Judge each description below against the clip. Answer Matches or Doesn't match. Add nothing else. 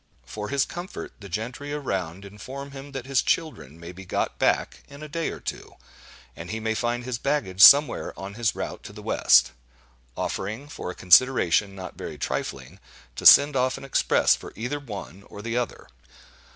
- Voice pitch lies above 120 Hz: Doesn't match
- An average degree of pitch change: Doesn't match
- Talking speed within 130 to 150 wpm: Doesn't match